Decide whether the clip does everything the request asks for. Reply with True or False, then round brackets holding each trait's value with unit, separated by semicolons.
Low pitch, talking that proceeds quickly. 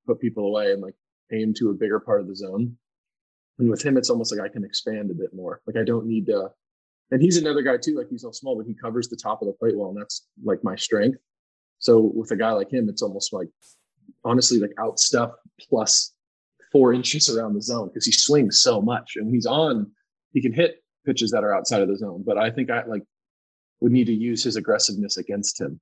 True (120 Hz; 240 wpm)